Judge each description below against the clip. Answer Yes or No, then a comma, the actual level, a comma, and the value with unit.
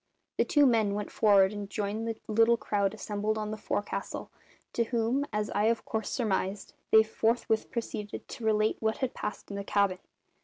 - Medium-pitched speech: No, high, 215 Hz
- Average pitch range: No, narrow, 1.8 semitones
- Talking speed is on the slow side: No, average, 185 wpm